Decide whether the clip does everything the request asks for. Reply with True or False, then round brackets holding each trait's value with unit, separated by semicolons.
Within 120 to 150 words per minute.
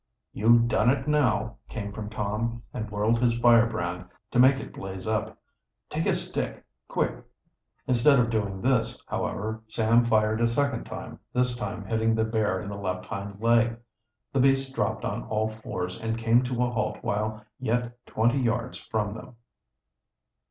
False (165 wpm)